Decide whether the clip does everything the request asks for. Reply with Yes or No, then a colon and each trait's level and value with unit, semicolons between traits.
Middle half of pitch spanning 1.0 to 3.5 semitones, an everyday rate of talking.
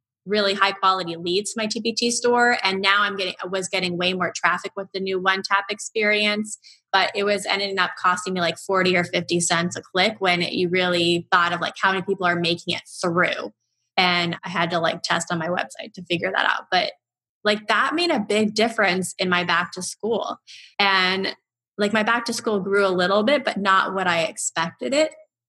No: average, 2.9 semitones; fast, 220 wpm